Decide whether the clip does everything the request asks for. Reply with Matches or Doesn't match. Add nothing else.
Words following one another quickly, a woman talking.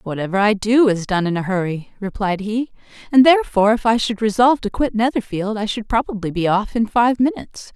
Matches